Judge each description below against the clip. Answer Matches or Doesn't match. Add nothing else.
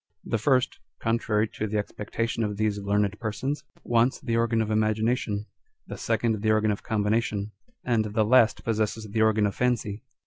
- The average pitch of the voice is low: Matches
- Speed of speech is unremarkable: Matches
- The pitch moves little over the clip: Matches